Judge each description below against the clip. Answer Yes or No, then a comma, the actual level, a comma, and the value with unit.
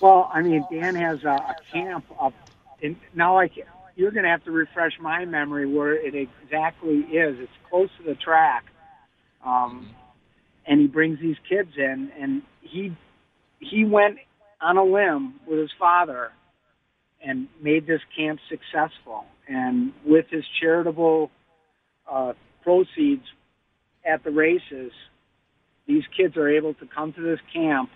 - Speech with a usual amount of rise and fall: Yes, average, 3.7 semitones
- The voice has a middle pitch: Yes, medium, 160 Hz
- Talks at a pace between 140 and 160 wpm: Yes, average, 150 wpm